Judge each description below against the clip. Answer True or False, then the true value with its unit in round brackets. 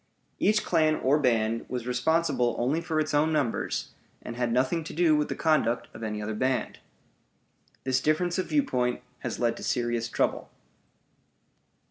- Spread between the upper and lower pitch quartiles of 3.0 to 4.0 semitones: False (4.8 semitones)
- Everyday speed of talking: True (160 wpm)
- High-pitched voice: False (130 Hz)